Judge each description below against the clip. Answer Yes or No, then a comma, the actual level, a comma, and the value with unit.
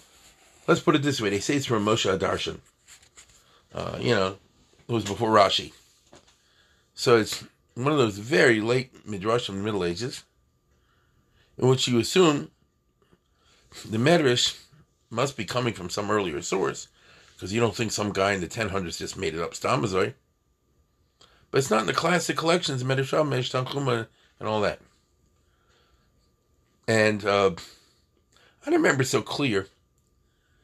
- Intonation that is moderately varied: Yes, average, 4.6 semitones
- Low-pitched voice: Yes, low, 110 Hz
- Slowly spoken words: No, average, 150 wpm